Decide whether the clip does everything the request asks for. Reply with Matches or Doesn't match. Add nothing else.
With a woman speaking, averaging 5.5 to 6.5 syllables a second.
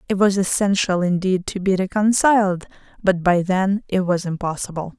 Doesn't match